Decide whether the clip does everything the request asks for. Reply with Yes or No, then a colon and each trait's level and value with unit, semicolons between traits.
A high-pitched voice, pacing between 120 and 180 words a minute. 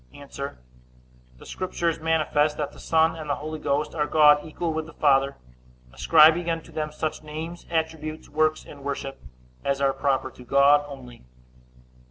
No: medium, 150 Hz; average, 160 wpm